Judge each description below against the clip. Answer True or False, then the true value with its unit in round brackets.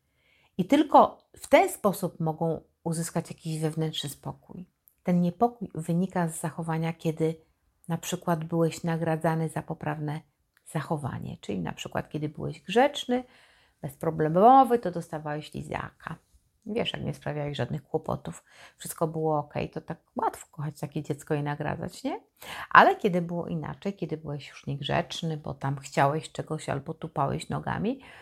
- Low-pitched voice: False (160 Hz)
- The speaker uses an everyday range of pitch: False (2.3 semitones)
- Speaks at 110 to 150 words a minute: True (140 wpm)